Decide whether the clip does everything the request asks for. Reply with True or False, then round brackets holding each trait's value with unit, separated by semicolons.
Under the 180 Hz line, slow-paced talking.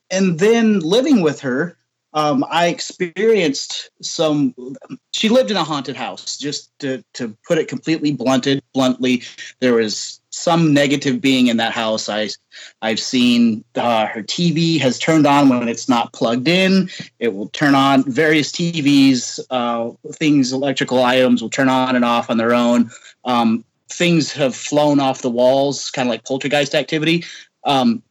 False (140 Hz; 160 wpm)